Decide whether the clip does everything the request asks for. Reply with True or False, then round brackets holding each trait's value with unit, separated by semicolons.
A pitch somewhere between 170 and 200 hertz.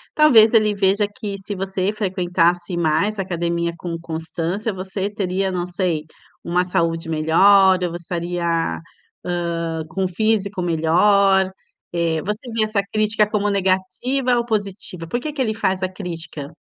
True (190 Hz)